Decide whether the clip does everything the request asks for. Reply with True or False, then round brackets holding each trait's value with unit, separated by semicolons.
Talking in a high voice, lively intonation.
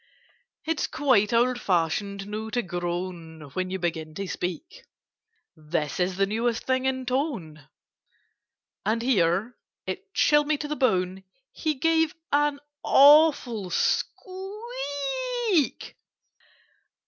True (230 Hz; 8.4 semitones)